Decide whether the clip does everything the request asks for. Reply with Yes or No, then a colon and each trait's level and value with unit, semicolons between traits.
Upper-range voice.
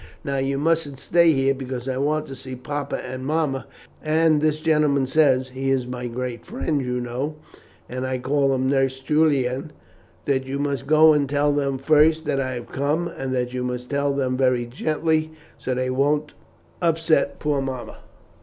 No: low, 135 Hz